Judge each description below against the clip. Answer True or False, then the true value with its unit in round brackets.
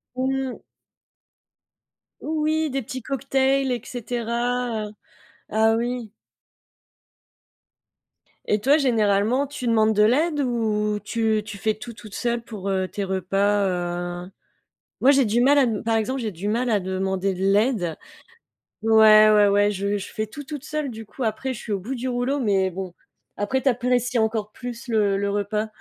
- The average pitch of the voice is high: True (225 Hz)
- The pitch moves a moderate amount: True (3.6 semitones)